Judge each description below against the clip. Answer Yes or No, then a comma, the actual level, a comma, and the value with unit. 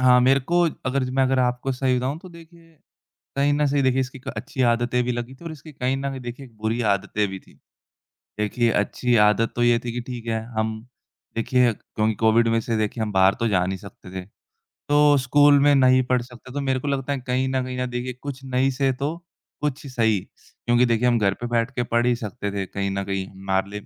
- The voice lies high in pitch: No, low, 125 Hz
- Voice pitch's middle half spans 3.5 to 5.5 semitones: No, average, 3.0 semitones